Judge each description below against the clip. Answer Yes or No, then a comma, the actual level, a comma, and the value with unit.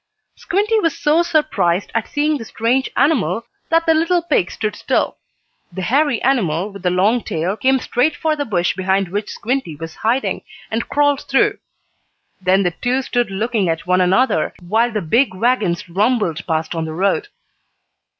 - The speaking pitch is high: Yes, high, 225 Hz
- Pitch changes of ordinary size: No, wide, 7.2 semitones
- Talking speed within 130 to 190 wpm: Yes, average, 170 wpm